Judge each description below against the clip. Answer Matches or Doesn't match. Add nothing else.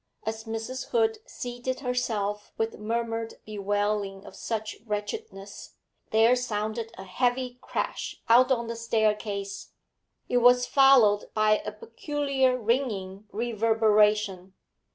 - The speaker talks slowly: Matches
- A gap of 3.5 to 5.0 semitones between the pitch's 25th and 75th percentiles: Doesn't match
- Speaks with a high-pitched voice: Matches